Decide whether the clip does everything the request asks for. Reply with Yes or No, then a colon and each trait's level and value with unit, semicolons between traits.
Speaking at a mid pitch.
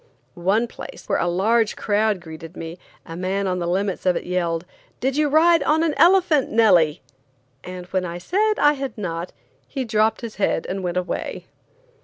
No: high, 195 Hz